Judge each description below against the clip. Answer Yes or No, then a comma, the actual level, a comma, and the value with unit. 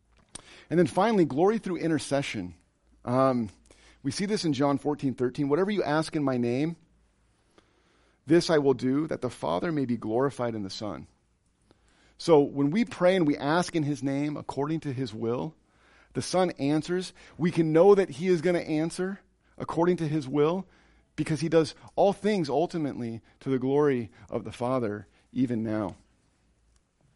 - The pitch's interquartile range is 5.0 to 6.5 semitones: Yes, wide, 5.5 semitones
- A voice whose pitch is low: No, medium, 145 Hz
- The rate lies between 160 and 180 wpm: Yes, average, 170 wpm